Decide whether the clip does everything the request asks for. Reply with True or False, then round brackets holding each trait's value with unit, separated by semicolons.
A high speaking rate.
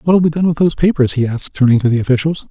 True (285 wpm)